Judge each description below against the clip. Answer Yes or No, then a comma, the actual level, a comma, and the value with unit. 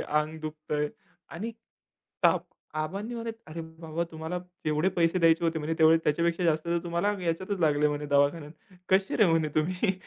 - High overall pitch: No, medium, 165 Hz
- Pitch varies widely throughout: No, narrow, 2.4 semitones